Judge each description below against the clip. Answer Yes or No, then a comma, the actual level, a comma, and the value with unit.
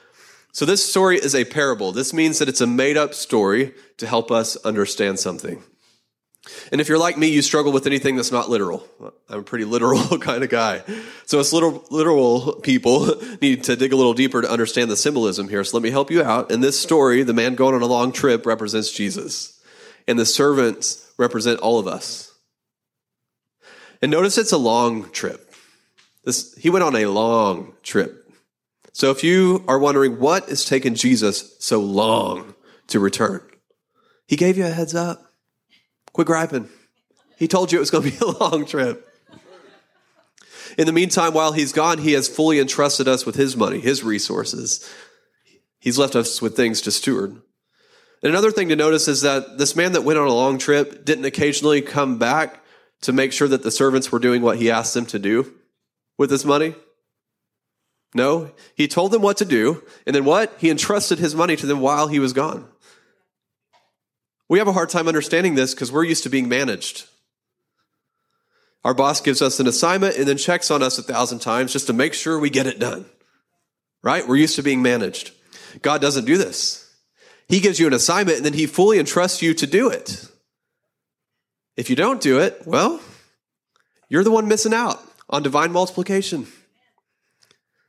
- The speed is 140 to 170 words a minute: No, average, 185 wpm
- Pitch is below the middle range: No, medium, 145 Hz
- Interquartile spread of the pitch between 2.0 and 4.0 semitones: No, average, 4.8 semitones